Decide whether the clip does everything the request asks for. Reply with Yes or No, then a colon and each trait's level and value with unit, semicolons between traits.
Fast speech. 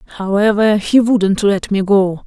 No: average, 160 wpm